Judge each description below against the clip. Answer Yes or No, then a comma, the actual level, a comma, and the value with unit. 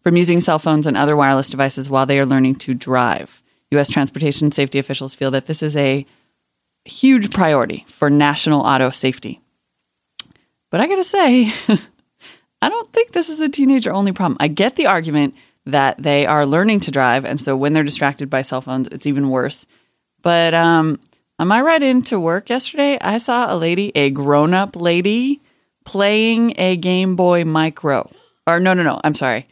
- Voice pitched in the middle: Yes, medium, 155 Hz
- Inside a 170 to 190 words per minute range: Yes, average, 180 wpm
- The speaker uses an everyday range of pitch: No, wide, 6.4 semitones